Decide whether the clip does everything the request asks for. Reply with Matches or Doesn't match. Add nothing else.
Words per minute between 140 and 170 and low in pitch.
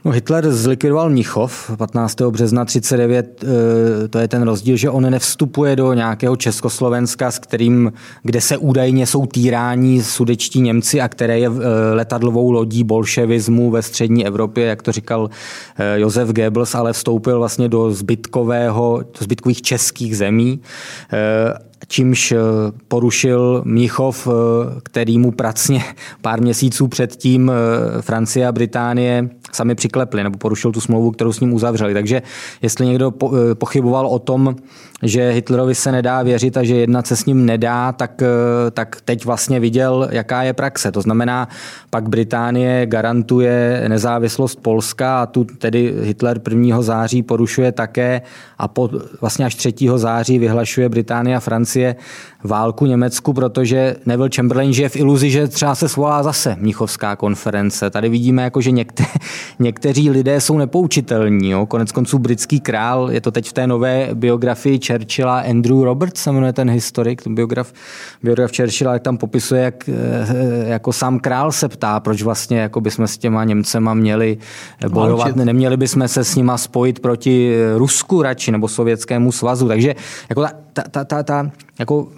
Matches